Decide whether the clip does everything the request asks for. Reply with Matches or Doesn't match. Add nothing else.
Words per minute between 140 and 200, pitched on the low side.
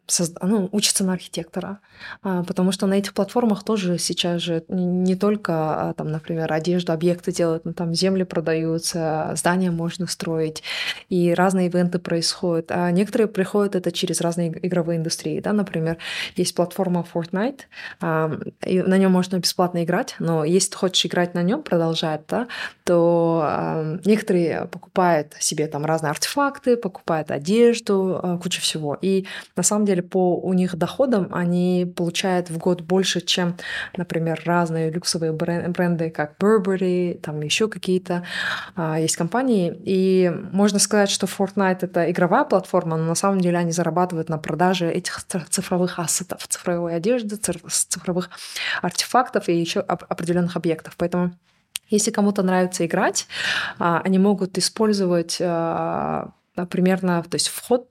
Doesn't match